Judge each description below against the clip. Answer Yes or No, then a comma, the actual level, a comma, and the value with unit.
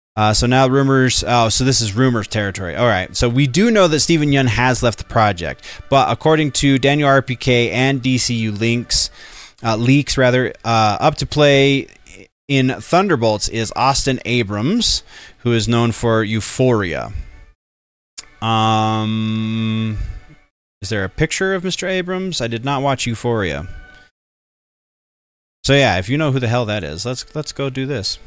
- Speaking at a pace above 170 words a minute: No, average, 160 wpm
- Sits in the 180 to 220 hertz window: No, low, 120 Hz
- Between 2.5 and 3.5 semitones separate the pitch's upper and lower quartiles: No, average, 4.0 semitones